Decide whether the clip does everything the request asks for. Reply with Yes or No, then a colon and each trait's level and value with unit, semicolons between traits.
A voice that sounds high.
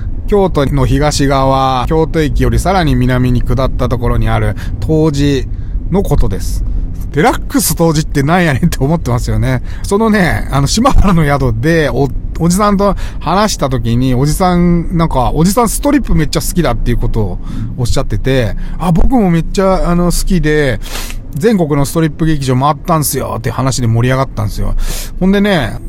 No: medium, 140 Hz